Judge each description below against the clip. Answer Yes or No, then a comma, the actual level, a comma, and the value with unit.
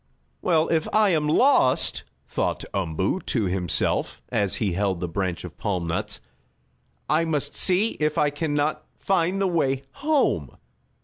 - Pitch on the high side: No, medium, 145 Hz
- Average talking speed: Yes, average, 150 wpm